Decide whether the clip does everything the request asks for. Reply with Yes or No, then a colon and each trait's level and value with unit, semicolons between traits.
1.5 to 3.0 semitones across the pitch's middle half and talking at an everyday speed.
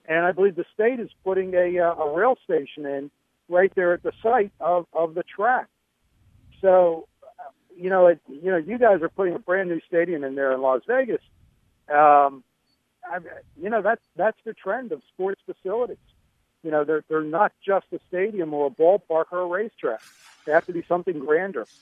No: average, 4.1 semitones; average, 195 wpm